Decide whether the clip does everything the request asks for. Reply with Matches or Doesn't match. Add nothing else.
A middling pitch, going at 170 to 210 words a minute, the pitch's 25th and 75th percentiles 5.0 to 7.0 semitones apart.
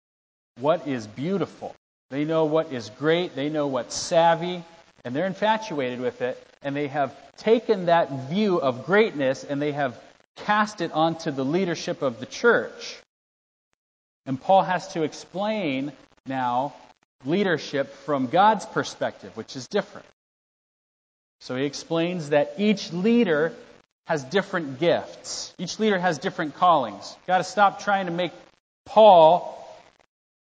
Doesn't match